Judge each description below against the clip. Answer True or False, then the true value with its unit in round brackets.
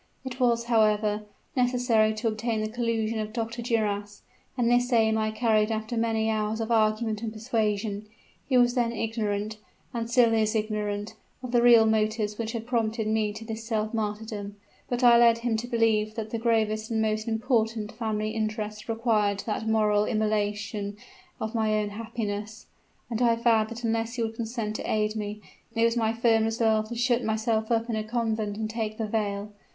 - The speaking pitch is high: True (220 Hz)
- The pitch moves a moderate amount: False (1.3 semitones)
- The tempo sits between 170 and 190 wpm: True (185 wpm)